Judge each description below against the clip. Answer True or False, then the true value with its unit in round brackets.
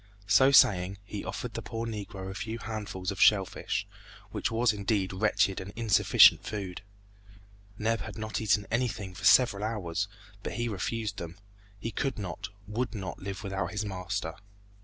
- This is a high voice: False (105 Hz)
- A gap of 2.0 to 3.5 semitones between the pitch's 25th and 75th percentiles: True (2.8 semitones)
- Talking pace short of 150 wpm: False (165 wpm)